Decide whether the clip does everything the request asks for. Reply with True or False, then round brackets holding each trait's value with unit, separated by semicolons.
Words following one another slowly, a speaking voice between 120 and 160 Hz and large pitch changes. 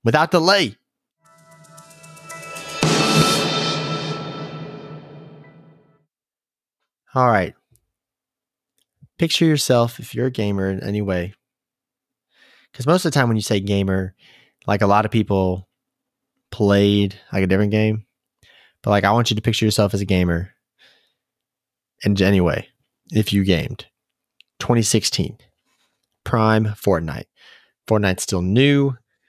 False (110 wpm; 110 Hz; 6.6 semitones)